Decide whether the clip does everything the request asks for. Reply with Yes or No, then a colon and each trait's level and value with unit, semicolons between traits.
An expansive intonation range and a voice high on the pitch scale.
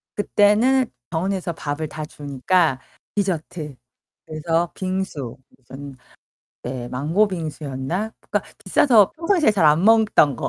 No: wide, 6.0 semitones; medium, 165 Hz